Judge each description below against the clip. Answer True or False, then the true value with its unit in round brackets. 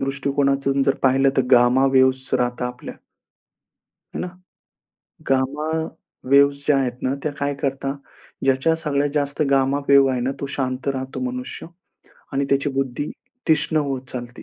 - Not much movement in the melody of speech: True (1.3 semitones)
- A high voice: False (135 Hz)